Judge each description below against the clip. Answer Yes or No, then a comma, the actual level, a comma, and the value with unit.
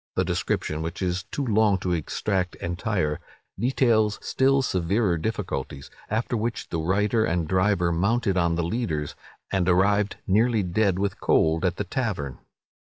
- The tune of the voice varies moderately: Yes, average, 4.2 semitones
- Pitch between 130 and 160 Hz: No, very low, 95 Hz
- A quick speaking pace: No, average, 150 wpm